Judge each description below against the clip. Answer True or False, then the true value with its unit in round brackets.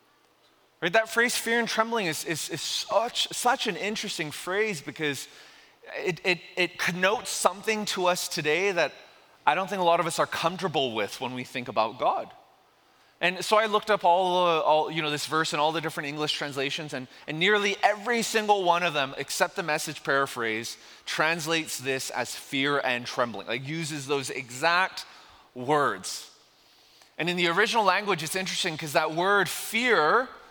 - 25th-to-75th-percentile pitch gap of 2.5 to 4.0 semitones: False (5.4 semitones)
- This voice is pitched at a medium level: True (170 Hz)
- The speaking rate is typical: True (180 wpm)